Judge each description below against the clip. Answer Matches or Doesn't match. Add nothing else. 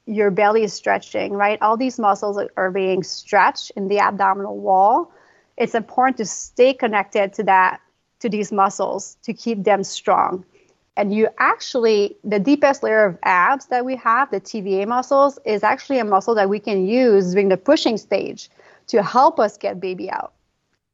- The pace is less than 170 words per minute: Doesn't match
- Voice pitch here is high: Matches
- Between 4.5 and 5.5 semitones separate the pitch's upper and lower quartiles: Doesn't match